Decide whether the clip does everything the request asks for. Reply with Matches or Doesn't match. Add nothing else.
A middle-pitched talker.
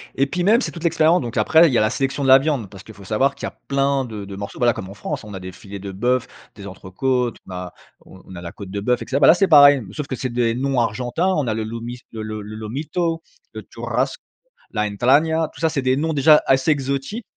Doesn't match